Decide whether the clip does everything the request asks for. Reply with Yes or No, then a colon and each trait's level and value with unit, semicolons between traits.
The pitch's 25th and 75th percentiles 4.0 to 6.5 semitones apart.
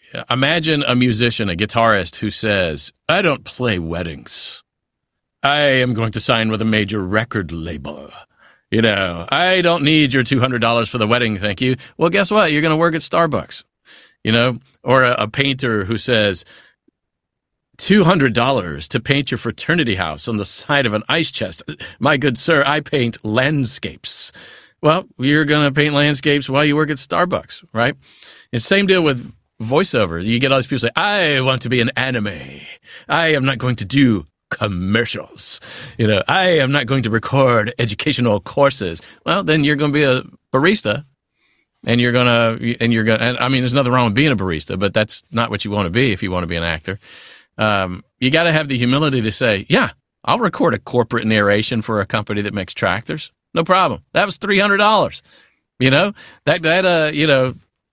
Yes: average, 5.1 semitones